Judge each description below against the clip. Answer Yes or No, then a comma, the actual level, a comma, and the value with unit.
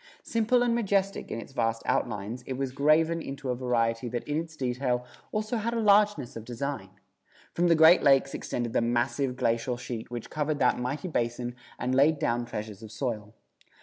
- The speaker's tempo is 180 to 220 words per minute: Yes, average, 185 wpm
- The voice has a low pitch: Yes, low, 130 Hz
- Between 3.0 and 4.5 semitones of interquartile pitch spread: No, average, 5.1 semitones